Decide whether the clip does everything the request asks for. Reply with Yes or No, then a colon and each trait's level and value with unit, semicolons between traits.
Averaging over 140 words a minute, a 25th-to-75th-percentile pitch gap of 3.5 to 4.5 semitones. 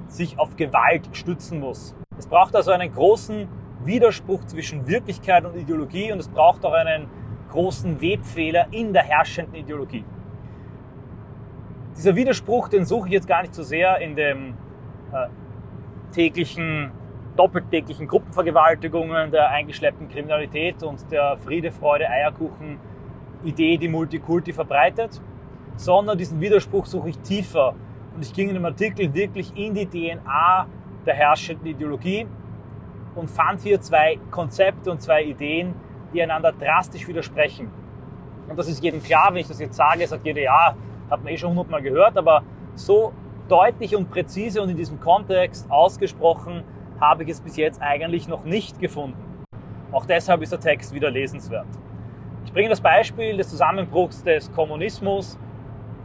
Yes: average, 150 wpm; average, 4.0 semitones